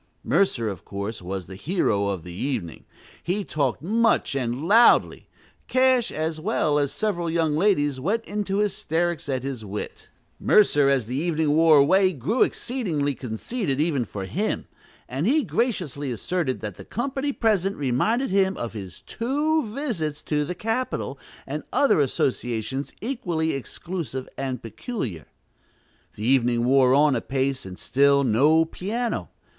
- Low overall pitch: No, medium, 150 Hz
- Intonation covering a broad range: Yes, wide, 7.6 semitones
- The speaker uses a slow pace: No, average, 145 wpm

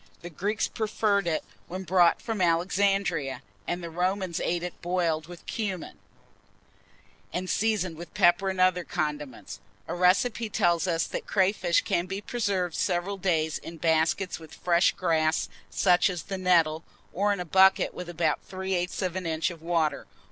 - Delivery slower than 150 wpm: No, average, 165 wpm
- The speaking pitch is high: No, medium, 180 Hz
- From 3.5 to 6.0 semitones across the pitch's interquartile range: No, narrow, 2.4 semitones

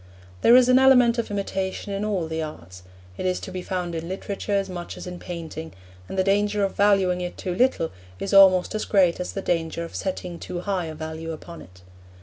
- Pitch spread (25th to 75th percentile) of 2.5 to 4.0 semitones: Yes, average, 3.1 semitones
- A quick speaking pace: Yes, fast, 220 wpm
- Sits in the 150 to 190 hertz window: Yes, medium, 185 Hz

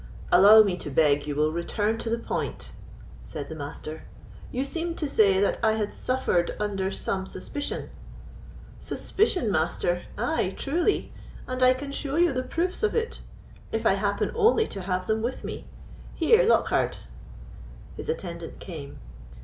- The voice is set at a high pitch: Yes, high, 220 Hz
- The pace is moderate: Yes, average, 155 wpm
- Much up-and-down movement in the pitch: Yes, wide, 8.3 semitones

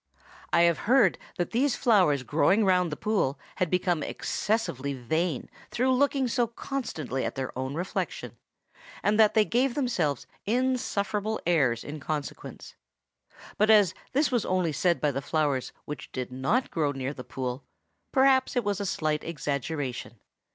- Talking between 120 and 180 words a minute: Yes, average, 155 wpm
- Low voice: No, medium, 175 Hz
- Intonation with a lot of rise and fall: Yes, wide, 7.8 semitones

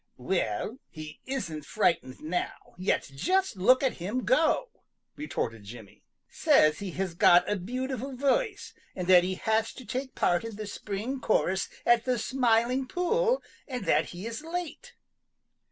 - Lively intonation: Yes, wide, 6.8 semitones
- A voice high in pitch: Yes, high, 225 Hz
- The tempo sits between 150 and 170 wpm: Yes, average, 155 wpm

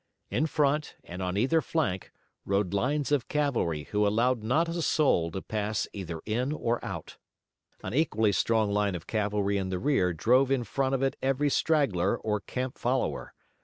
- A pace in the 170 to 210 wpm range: Yes, average, 175 wpm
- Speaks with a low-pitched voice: Yes, low, 115 Hz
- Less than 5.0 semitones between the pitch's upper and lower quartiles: No, wide, 5.6 semitones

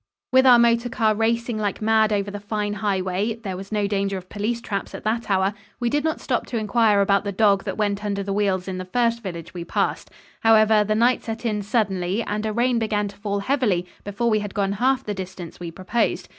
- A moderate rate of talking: No, fast, 230 wpm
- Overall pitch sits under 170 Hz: No, high, 210 Hz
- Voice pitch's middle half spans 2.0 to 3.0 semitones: Yes, narrow, 2.6 semitones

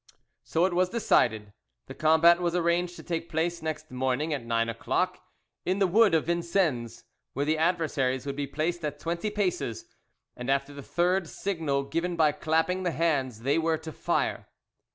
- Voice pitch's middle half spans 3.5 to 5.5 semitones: Yes, average, 3.9 semitones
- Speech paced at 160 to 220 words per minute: Yes, average, 175 wpm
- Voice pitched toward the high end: No, medium, 160 Hz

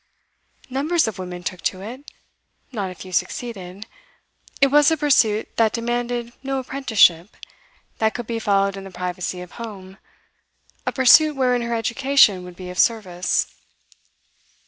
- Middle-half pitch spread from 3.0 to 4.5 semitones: No, wide, 5.4 semitones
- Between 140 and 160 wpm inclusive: Yes, average, 145 wpm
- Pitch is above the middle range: Yes, high, 225 Hz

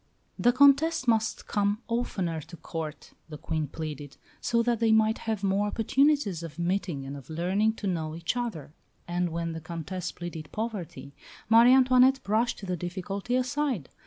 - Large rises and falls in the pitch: Yes, wide, 6.1 semitones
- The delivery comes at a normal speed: Yes, average, 160 wpm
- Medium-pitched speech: No, high, 195 Hz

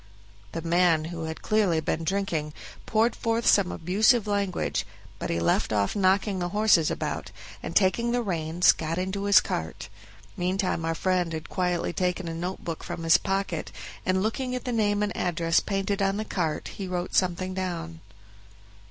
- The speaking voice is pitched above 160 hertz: Yes, medium, 185 Hz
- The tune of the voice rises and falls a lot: No, average, 3.4 semitones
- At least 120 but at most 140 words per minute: No, average, 175 wpm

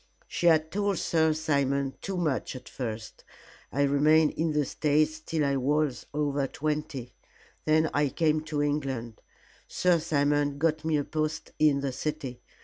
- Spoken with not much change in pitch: Yes, narrow, 2.0 semitones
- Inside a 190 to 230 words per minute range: No, average, 155 wpm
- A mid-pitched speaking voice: Yes, medium, 150 Hz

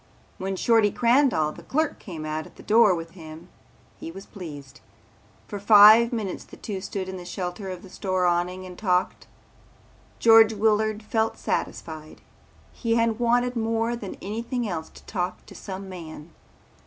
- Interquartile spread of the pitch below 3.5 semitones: No, average, 4.1 semitones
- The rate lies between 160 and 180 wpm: Yes, average, 165 wpm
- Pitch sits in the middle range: No, high, 195 Hz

